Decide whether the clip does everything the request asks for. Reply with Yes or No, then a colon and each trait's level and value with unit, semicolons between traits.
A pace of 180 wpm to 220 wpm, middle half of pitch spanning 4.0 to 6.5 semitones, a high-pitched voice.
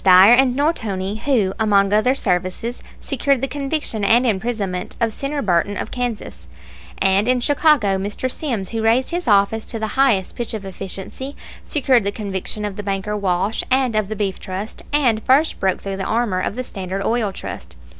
Yes: average, 185 wpm; average, 4.5 semitones; high, 215 Hz